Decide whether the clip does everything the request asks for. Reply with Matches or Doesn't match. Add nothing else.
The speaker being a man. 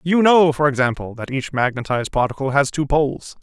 Matches